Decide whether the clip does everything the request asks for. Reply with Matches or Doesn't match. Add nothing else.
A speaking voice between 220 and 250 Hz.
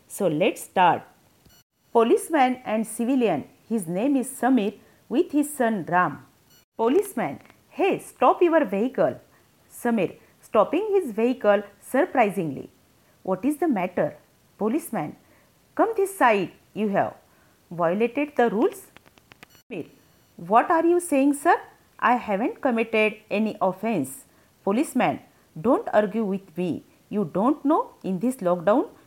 Matches